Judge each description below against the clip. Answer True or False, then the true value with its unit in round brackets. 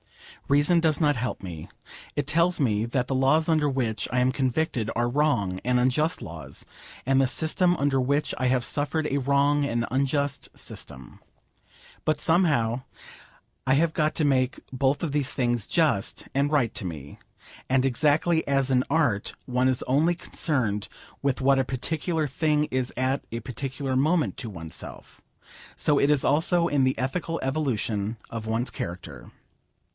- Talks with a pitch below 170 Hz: True (135 Hz)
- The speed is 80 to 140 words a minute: False (165 wpm)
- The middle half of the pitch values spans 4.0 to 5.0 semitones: False (3.4 semitones)